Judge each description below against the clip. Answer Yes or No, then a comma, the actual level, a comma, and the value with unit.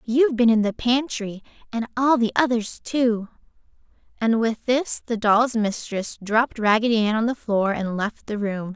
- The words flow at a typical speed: Yes, average, 180 wpm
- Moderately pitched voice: No, high, 225 Hz